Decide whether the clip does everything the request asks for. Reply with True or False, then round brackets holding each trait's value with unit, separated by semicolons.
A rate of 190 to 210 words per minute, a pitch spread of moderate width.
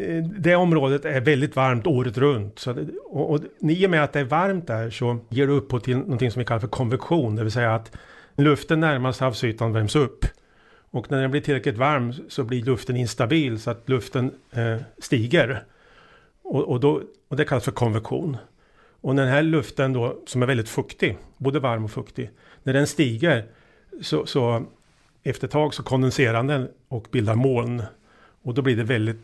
True (195 wpm; 3.4 semitones)